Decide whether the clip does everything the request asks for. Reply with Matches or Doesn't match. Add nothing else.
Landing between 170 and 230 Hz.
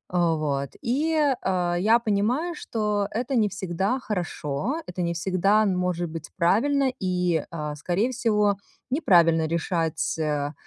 Matches